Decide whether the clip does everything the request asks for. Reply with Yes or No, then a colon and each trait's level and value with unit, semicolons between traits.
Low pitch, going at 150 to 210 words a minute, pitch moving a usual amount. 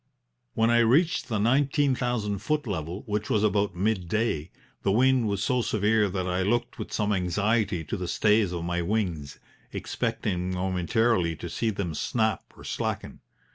Yes: low, 105 Hz; average, 165 wpm; average, 4.0 semitones